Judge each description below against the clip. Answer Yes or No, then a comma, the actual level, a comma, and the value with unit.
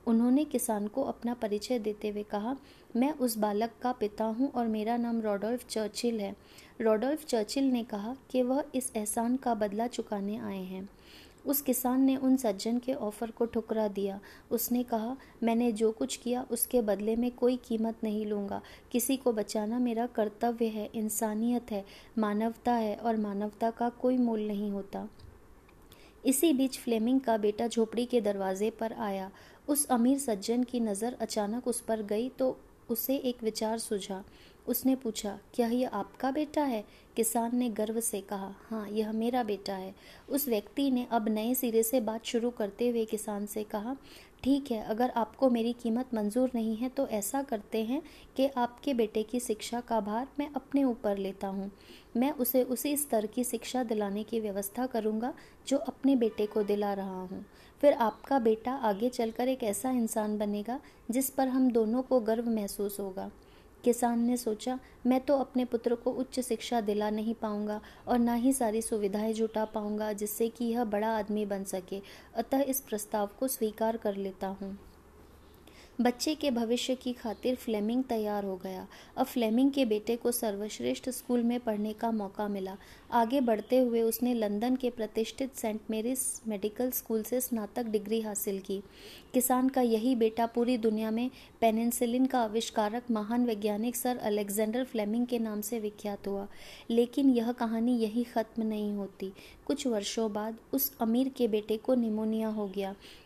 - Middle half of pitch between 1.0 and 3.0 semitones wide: Yes, narrow, 2.6 semitones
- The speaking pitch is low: No, high, 230 Hz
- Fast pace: No, average, 175 wpm